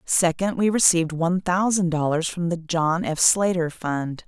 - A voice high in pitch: No, medium, 170 Hz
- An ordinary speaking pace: Yes, average, 170 wpm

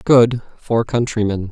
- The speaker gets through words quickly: No, slow, 120 wpm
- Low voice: Yes, low, 115 Hz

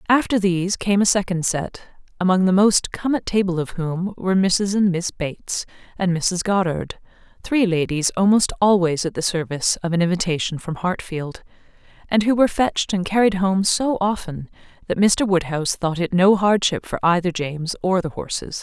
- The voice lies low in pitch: No, medium, 185 Hz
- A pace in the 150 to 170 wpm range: No, average, 180 wpm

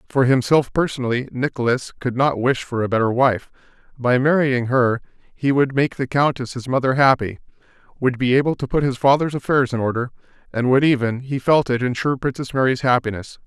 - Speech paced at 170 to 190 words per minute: Yes, average, 180 wpm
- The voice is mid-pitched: No, low, 130 Hz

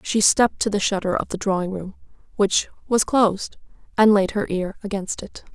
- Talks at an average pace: Yes, average, 195 wpm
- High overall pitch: Yes, high, 200 Hz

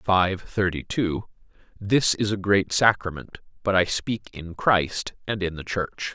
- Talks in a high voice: No, very low, 95 Hz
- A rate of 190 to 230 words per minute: No, average, 165 wpm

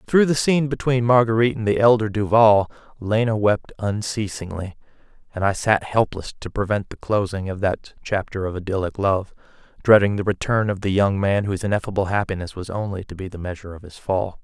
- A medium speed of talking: Yes, average, 185 wpm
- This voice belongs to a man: Yes, male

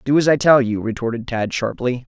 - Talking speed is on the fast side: Yes, fast, 225 wpm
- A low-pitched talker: Yes, low, 125 Hz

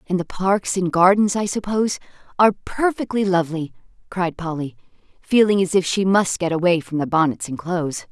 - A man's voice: No, female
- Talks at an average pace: Yes, average, 180 wpm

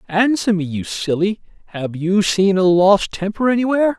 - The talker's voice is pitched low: No, high, 195 Hz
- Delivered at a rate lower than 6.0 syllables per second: Yes, 4.9 syllables/s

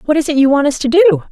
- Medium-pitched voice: No, very high, 290 Hz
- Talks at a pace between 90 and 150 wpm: No, fast, 365 wpm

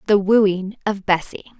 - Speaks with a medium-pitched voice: No, high, 200 Hz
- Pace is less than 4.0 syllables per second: No, 4.2 syllables/s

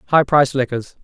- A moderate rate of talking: Yes, average, 175 wpm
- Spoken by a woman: No, male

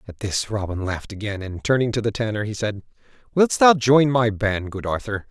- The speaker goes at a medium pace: No, fast, 215 wpm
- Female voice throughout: No, male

